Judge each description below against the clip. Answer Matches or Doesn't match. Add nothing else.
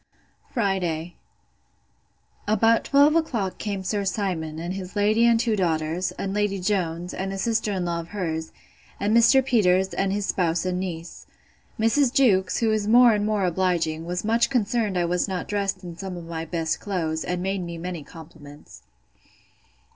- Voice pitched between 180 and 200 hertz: Matches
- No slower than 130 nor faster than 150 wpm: Doesn't match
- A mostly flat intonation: Doesn't match